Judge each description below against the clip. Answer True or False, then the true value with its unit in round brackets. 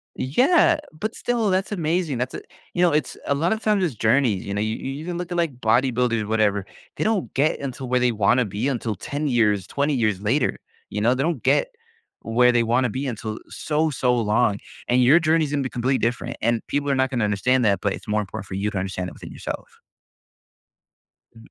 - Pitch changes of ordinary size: False (5.7 semitones)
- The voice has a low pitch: True (125 Hz)